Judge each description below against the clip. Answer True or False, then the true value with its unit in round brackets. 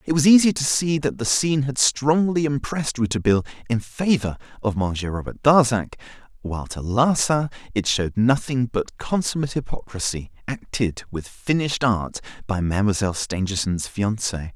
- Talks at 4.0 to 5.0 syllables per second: False (5.4 syllables/s)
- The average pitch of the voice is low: True (120 Hz)